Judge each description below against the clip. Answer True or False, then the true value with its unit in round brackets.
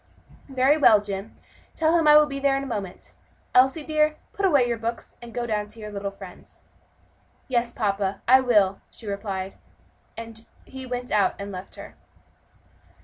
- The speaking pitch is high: True (235 Hz)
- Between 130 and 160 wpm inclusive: False (175 wpm)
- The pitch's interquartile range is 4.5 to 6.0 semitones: True (4.8 semitones)